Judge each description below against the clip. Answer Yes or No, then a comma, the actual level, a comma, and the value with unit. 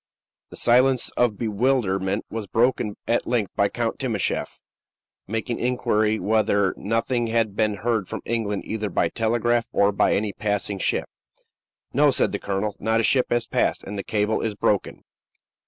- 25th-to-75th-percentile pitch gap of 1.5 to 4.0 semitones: Yes, narrow, 2.6 semitones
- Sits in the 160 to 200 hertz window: No, low, 110 Hz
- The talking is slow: No, average, 160 wpm